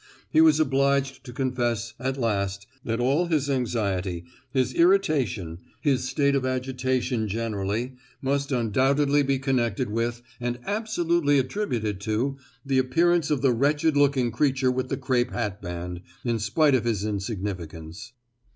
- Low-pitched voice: Yes, low, 130 Hz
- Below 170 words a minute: Yes, average, 140 wpm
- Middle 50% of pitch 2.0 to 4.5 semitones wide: Yes, average, 4.0 semitones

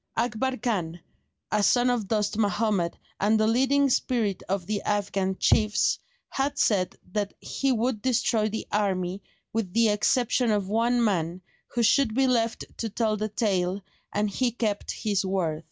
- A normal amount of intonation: Yes, average, 3.0 semitones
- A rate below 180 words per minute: Yes, average, 160 wpm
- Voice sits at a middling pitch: No, high, 215 Hz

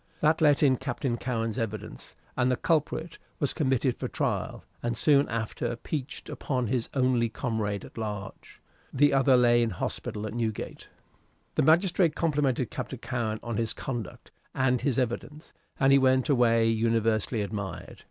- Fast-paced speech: No, average, 160 wpm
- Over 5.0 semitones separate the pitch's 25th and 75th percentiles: No, average, 3.3 semitones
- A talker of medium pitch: No, low, 125 Hz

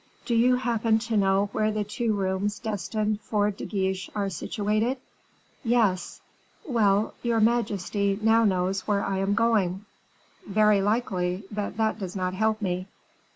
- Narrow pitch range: Yes, narrow, 2.3 semitones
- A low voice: No, high, 210 Hz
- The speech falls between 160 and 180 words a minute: No, average, 150 wpm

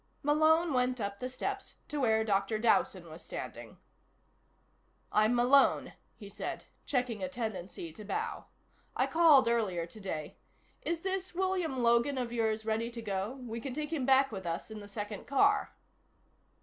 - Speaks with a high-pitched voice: Yes, high, 235 Hz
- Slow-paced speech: No, average, 160 wpm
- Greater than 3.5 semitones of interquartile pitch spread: Yes, average, 4.8 semitones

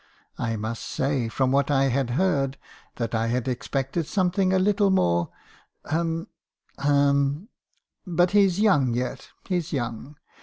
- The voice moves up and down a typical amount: No, wide, 5.9 semitones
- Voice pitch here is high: No, medium, 140 Hz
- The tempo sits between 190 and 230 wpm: No, average, 150 wpm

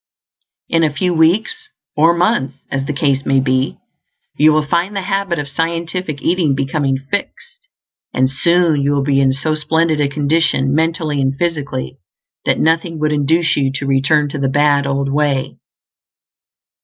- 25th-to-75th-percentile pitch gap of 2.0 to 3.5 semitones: Yes, average, 3.2 semitones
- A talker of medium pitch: Yes, medium, 150 Hz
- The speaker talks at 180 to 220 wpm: No, average, 165 wpm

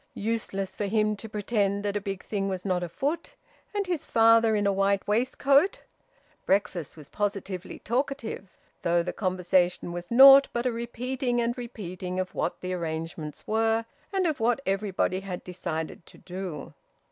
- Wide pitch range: No, average, 4.3 semitones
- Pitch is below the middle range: No, high, 200 Hz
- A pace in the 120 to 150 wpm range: No, average, 160 wpm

